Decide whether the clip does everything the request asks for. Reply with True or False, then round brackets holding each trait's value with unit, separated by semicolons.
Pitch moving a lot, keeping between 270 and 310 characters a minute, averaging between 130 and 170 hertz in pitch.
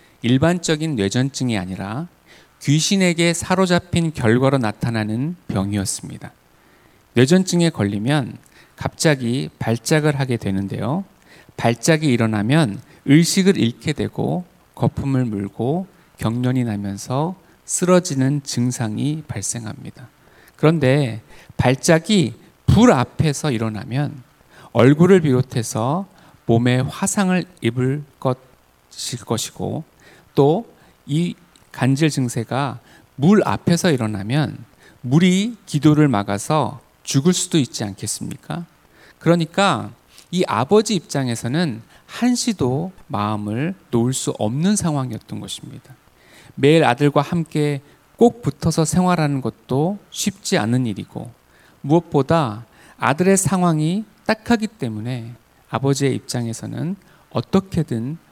False (6.1 semitones; 250 characters per minute; 140 Hz)